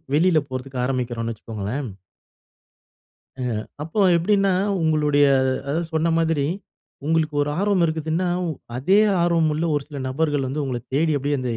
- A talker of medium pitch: Yes, medium, 150 Hz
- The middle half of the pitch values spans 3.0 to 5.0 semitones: Yes, average, 3.5 semitones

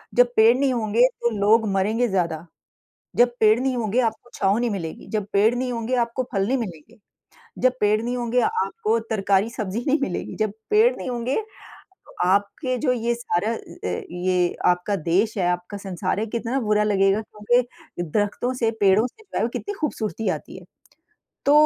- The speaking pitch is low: No, high, 225 Hz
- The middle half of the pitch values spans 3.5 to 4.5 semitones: Yes, average, 3.9 semitones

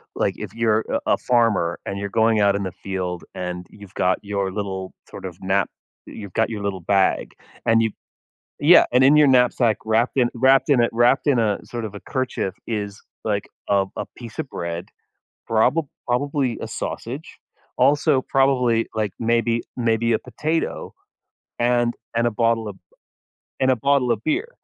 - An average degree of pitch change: Yes, average, 3.8 semitones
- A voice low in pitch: Yes, low, 115 Hz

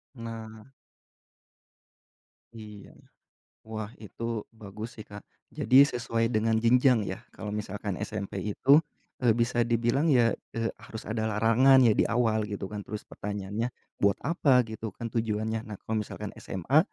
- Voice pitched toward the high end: No, low, 110 Hz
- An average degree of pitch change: No, narrow, 1.9 semitones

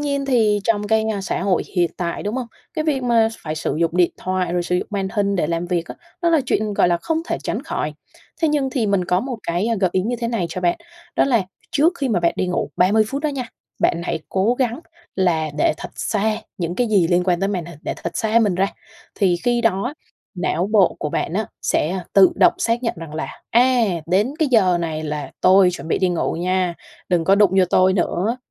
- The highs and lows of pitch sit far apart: No, average, 4.8 semitones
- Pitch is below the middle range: No, high, 195 Hz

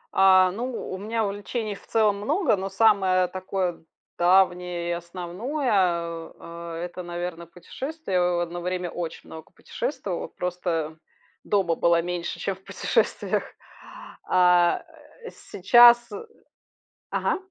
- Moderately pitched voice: Yes, medium, 180 Hz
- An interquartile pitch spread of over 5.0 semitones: No, average, 2.9 semitones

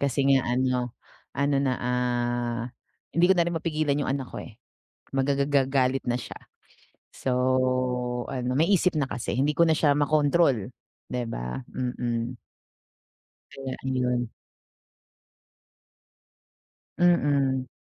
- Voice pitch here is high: No, low, 135 Hz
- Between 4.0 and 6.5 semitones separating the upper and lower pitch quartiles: No, average, 2.8 semitones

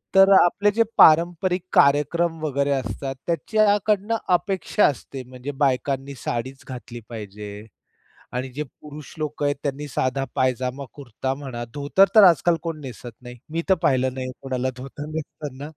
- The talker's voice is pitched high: No, medium, 140 Hz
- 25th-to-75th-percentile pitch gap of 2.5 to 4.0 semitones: No, average, 4.5 semitones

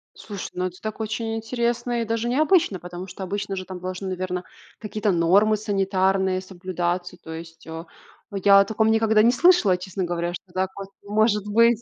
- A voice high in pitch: Yes, high, 195 Hz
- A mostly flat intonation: No, average, 3.2 semitones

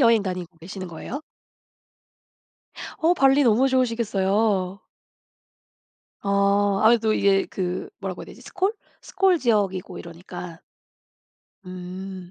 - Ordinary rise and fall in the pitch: Yes, average, 4.0 semitones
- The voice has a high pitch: Yes, high, 200 Hz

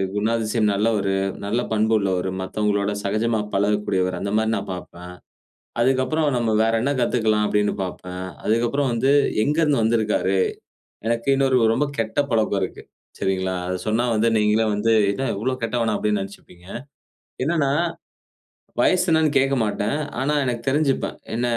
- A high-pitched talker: No, low, 110 Hz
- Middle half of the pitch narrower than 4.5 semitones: Yes, average, 4.0 semitones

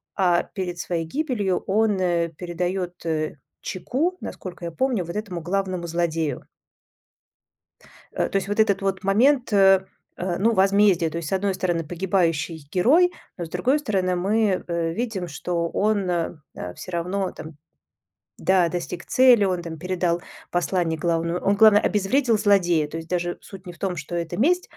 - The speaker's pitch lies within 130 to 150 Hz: No, medium, 185 Hz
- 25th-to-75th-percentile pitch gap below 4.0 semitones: Yes, average, 2.9 semitones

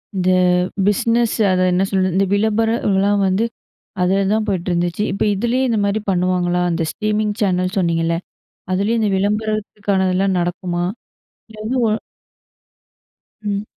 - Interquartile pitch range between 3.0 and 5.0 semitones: No, narrow, 2.6 semitones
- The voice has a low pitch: No, high, 195 Hz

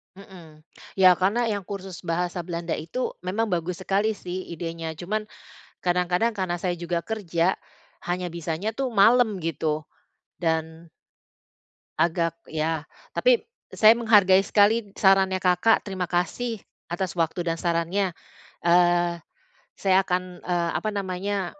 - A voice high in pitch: No, medium, 180 Hz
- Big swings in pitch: No, average, 2.9 semitones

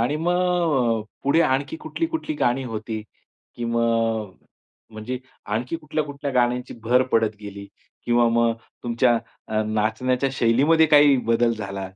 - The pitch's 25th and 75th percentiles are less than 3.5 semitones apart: No, average, 4.1 semitones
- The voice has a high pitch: No, low, 120 Hz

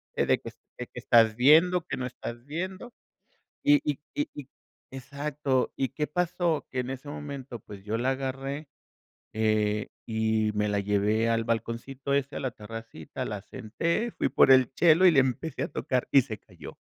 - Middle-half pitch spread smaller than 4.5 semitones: No, average, 4.8 semitones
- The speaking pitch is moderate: No, low, 130 Hz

